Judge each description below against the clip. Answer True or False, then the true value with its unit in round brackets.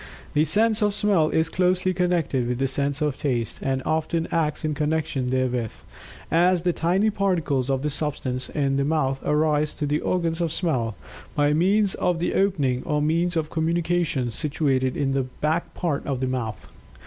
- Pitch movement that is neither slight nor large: True (4.3 semitones)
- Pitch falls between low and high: True (150 Hz)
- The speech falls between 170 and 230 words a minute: True (180 wpm)